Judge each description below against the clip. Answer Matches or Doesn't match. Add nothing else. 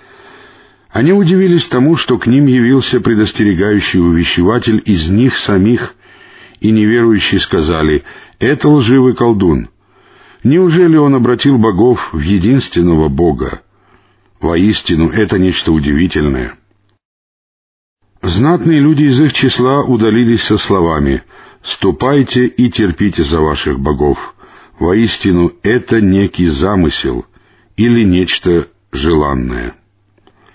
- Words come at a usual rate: Doesn't match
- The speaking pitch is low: Matches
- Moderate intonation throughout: Doesn't match